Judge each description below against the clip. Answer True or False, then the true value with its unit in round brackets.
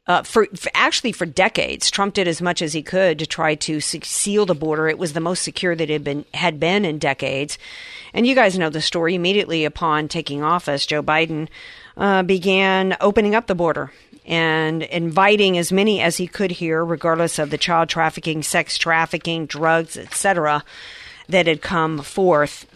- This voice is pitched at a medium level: True (170 Hz)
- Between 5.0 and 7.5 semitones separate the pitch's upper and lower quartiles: False (3.2 semitones)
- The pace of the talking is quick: False (185 wpm)